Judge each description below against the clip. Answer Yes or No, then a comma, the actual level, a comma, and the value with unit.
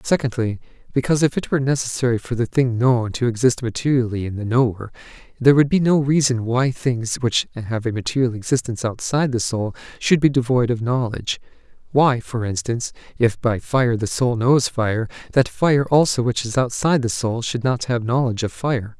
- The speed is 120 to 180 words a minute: No, average, 190 wpm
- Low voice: Yes, low, 125 Hz